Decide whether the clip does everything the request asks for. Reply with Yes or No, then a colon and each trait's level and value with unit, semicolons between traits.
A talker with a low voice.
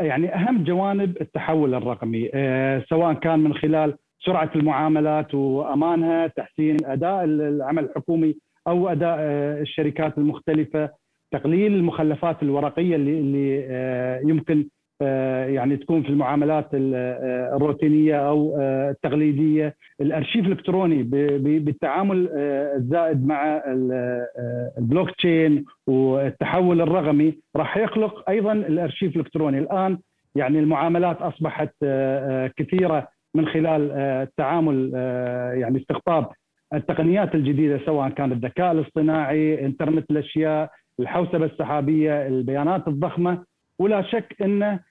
No: medium, 155 Hz